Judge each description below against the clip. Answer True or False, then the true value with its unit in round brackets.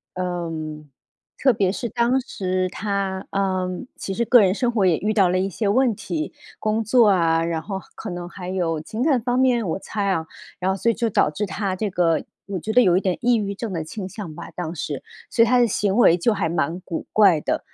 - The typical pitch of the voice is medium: False (195 Hz)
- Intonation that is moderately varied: True (4.0 semitones)